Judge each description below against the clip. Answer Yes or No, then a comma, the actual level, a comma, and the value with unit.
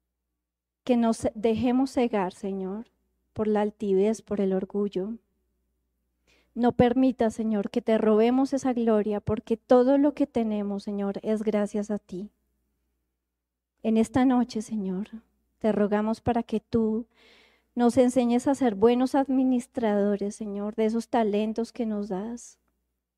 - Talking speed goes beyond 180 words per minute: No, average, 130 wpm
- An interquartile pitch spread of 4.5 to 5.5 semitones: No, average, 3.0 semitones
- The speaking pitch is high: Yes, high, 220 Hz